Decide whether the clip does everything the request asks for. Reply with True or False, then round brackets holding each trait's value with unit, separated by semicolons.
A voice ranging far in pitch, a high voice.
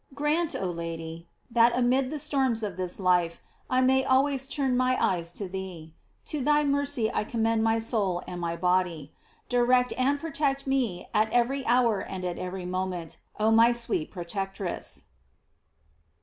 True (6.4 semitones; 225 Hz)